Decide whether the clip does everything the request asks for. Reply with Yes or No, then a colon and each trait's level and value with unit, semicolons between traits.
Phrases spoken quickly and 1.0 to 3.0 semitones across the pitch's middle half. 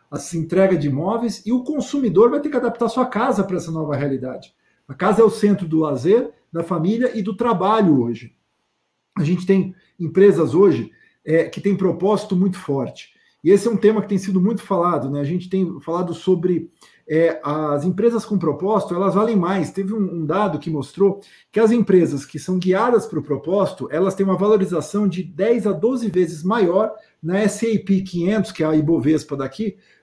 No: fast, 195 wpm; average, 4.2 semitones